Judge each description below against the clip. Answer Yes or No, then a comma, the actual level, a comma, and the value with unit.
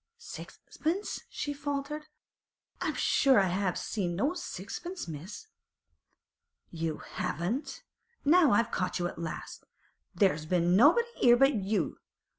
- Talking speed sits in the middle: No, slow, 120 wpm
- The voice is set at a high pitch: Yes, high, 215 Hz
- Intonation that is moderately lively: No, wide, 8.7 semitones